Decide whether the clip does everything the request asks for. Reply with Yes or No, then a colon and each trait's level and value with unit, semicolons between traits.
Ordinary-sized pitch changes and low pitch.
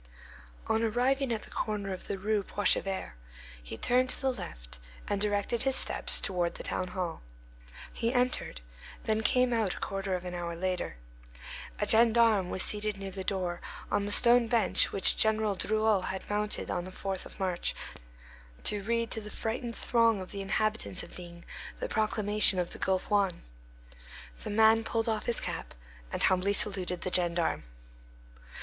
No: average, 3.2 semitones; high, 205 Hz